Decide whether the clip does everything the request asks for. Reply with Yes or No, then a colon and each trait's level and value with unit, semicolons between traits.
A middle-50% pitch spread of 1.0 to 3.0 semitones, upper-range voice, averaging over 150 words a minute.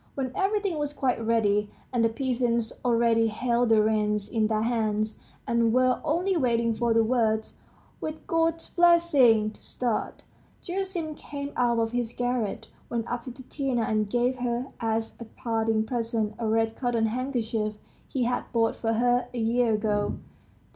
Yes: narrow, 2.4 semitones; high, 235 Hz; average, 160 wpm